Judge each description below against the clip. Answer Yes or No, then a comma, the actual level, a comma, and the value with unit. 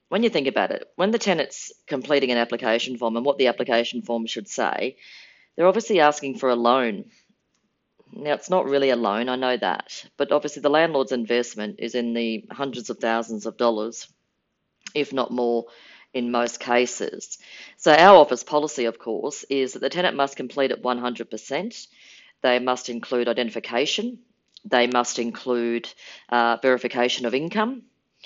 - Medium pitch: No, low, 125 Hz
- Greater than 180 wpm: No, average, 165 wpm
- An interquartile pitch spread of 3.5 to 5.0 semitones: No, average, 2.8 semitones